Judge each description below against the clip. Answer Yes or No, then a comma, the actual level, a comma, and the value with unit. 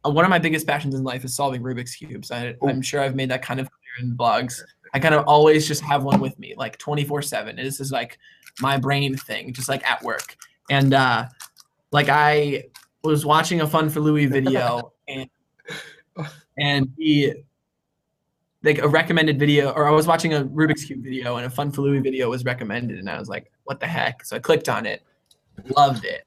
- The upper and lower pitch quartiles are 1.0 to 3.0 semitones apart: Yes, narrow, 2.5 semitones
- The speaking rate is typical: No, fast, 210 wpm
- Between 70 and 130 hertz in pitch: No, medium, 140 Hz